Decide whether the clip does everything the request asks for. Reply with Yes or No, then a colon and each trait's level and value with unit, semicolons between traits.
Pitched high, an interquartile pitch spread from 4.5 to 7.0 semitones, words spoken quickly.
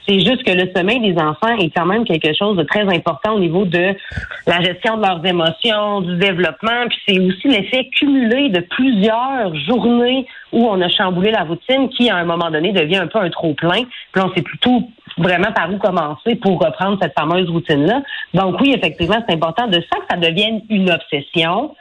No: high, 195 Hz; average, 4.8 semitones; average, 205 wpm